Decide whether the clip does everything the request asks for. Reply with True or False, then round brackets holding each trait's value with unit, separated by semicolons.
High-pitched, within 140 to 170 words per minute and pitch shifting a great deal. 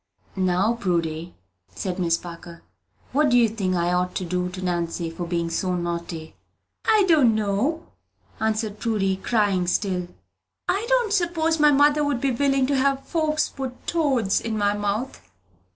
True (210 Hz; 160 wpm; 7.5 semitones)